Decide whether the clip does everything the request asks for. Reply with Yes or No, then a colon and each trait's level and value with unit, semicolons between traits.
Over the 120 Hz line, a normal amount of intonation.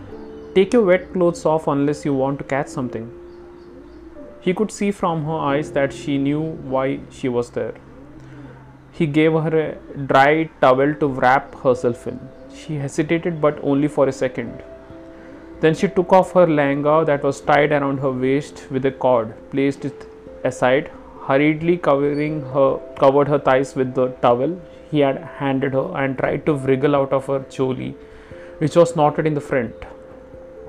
Yes: medium, 140 Hz; average, 3.1 semitones